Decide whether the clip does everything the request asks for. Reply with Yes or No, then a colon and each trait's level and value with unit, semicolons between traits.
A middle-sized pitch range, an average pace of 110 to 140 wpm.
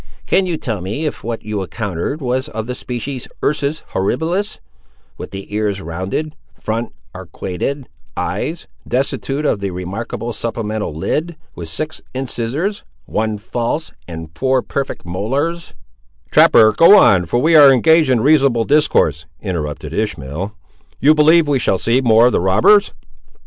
No: wide, 7.0 semitones; slow, 135 wpm